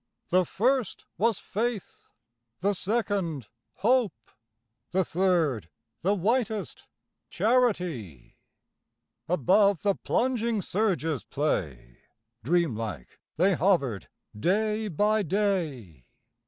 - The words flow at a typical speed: No, slow, 85 wpm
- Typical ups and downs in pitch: No, wide, 6.7 semitones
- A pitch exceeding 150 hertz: Yes, medium, 185 Hz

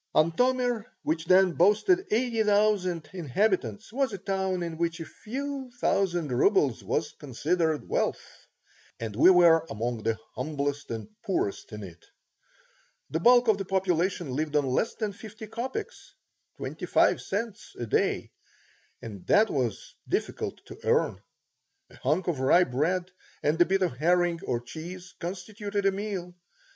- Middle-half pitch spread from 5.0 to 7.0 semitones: Yes, wide, 5.6 semitones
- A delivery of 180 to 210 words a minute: No, average, 150 wpm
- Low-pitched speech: No, medium, 180 Hz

